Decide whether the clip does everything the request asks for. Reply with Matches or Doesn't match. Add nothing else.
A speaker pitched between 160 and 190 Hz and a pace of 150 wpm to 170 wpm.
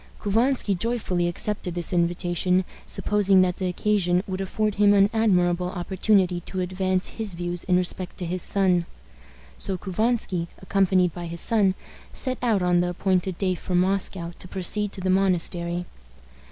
Matches